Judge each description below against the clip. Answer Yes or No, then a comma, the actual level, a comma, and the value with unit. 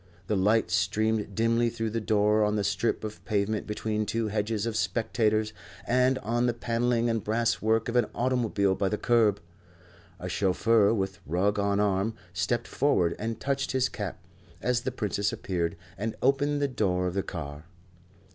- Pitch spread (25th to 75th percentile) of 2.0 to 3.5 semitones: Yes, narrow, 2.6 semitones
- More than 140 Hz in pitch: No, low, 110 Hz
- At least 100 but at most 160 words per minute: No, average, 175 wpm